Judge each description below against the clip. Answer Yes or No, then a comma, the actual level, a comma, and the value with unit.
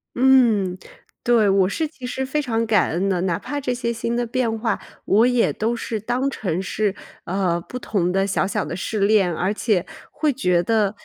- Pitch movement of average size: Yes, average, 4.1 semitones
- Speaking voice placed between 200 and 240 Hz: Yes, high, 220 Hz